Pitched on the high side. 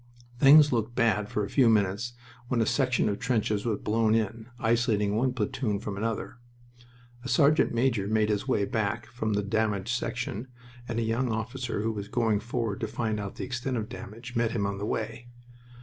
No: low, 110 Hz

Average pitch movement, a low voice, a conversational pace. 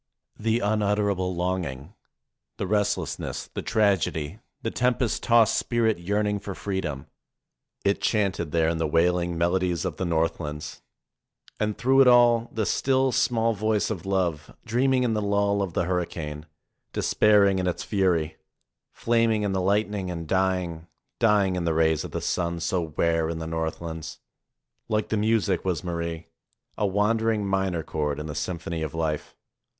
Yes: average, 4.3 semitones; very low, 95 Hz; average, 160 wpm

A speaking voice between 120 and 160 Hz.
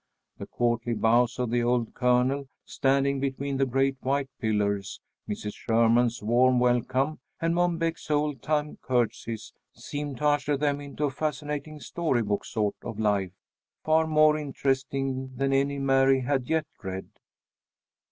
Yes: low, 135 Hz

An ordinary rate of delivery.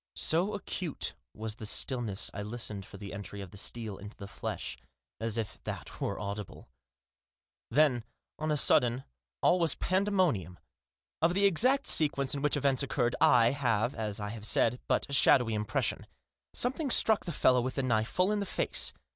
Yes: average, 180 wpm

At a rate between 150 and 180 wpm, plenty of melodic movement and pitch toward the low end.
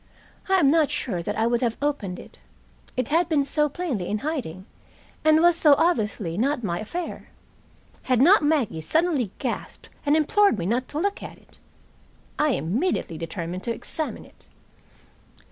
No: average, 165 wpm; wide, 7.2 semitones; very high, 275 Hz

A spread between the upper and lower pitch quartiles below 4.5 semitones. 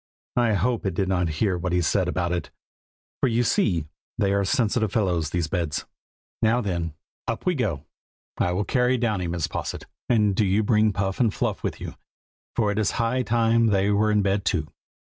Yes: average, 4.1 semitones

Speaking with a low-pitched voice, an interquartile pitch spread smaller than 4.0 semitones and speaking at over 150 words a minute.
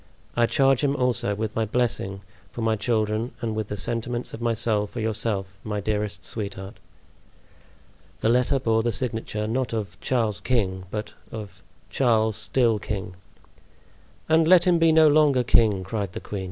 Yes: low, 110 Hz; average, 2.9 semitones; average, 165 wpm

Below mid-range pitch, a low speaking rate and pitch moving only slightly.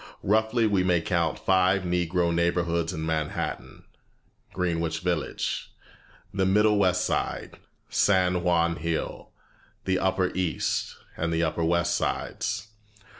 Yes: very low, 90 Hz; slow, 120 wpm; narrow, 2.0 semitones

